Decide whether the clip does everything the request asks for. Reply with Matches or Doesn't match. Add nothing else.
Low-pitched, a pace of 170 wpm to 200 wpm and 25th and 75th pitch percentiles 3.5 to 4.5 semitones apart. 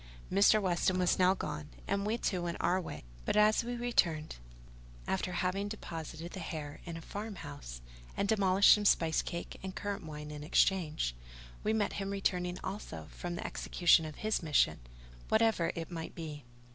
Doesn't match